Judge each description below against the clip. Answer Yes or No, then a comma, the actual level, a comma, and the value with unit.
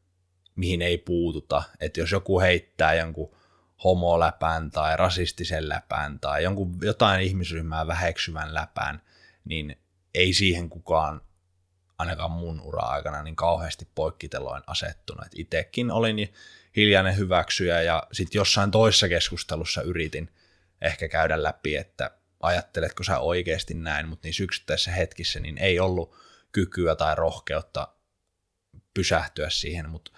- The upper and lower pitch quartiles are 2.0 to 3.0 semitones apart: Yes, narrow, 2.4 semitones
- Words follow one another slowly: No, average, 115 wpm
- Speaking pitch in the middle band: No, very low, 90 Hz